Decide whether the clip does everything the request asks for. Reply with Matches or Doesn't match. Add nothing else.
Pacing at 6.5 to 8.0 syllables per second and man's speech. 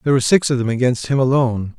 Matches